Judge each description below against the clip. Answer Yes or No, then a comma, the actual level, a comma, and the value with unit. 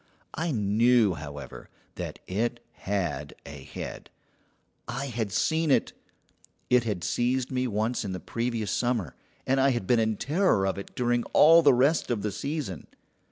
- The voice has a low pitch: Yes, low, 120 Hz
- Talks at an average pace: Yes, average, 160 wpm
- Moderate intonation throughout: Yes, average, 4.7 semitones